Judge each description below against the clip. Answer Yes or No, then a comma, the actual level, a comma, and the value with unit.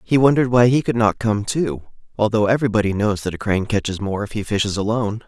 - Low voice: Yes, low, 110 Hz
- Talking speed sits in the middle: No, fast, 230 wpm